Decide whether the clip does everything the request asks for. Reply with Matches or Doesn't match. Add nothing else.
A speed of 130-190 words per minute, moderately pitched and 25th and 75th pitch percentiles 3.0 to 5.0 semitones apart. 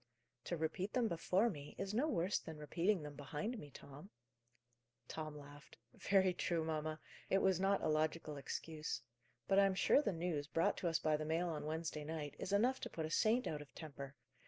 Doesn't match